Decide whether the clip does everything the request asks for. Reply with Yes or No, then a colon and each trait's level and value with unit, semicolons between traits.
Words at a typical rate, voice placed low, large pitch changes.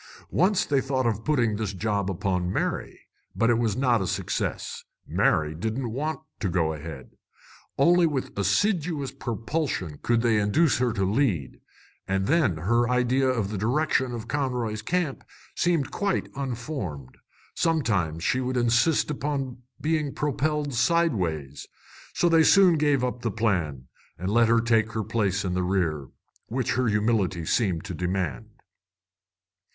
Yes: average, 150 wpm; low, 115 Hz; wide, 6.3 semitones